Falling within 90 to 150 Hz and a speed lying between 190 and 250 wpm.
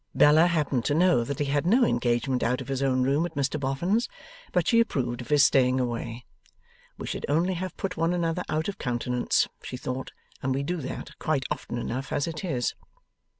Yes: medium, 140 Hz; fast, 205 wpm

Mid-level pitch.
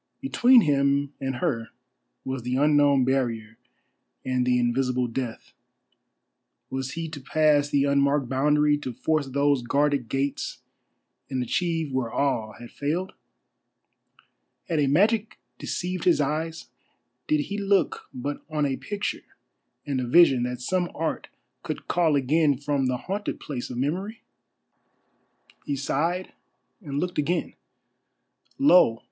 Yes: medium, 145 Hz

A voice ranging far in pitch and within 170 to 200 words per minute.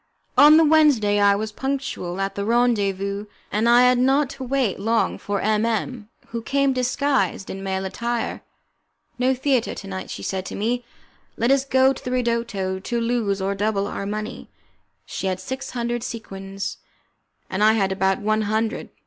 No: average, 4.1 semitones; average, 175 wpm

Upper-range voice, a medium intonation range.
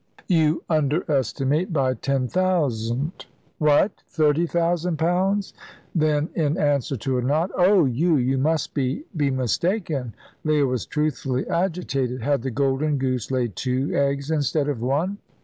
No: medium, 145 Hz; average, 3.9 semitones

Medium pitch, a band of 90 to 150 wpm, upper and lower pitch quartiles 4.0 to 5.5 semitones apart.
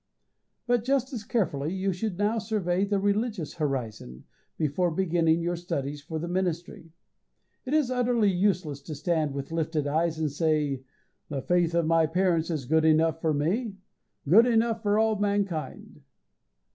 No: medium, 170 Hz; average, 160 wpm; average, 4.8 semitones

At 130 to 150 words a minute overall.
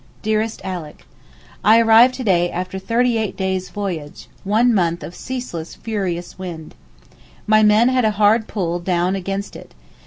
No: average, 160 wpm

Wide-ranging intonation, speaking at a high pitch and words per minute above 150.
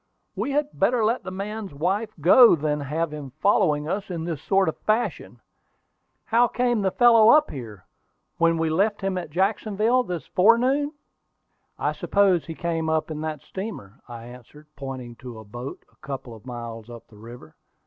No: wide, 7.9 semitones; medium, 165 Hz; average, 180 wpm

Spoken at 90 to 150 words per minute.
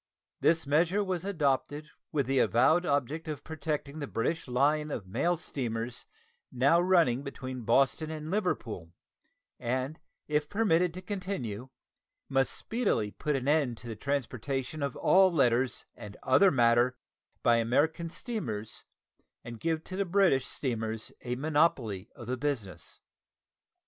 Yes: slow, 135 wpm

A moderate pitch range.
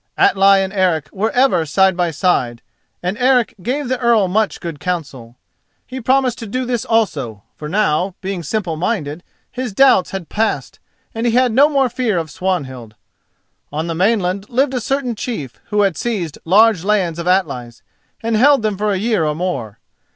No: wide, 5.9 semitones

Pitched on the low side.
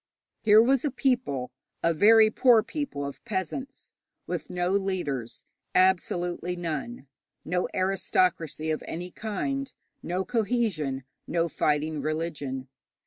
No: medium, 180 Hz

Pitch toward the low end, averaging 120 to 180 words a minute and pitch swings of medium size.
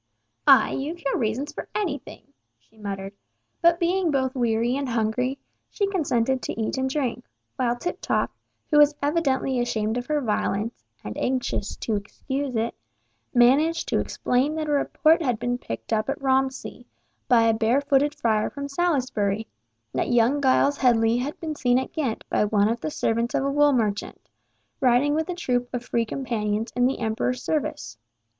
No: very high, 255 Hz; average, 170 wpm; average, 4.1 semitones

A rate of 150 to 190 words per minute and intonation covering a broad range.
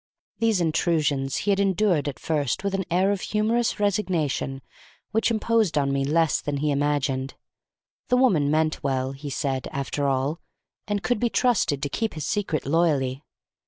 Yes: average, 165 wpm; wide, 6.4 semitones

